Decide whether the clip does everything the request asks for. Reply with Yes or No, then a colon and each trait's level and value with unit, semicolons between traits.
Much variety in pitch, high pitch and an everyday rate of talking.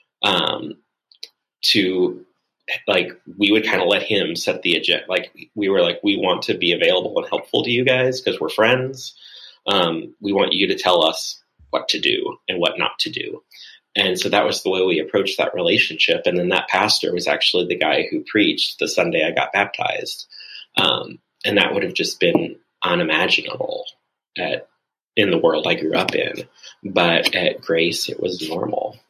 Yes: wide, 7.5 semitones; very high, 390 Hz; average, 190 wpm